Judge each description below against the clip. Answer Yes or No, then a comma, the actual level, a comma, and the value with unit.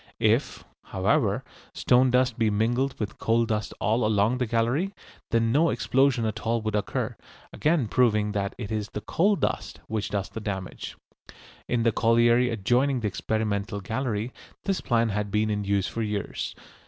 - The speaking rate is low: No, average, 165 wpm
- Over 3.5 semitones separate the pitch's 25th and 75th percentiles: No, average, 2.9 semitones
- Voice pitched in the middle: No, low, 115 Hz